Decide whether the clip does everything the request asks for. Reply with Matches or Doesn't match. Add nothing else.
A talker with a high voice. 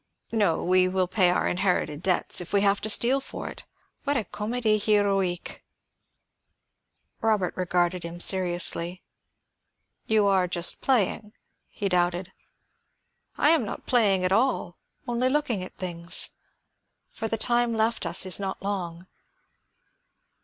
Matches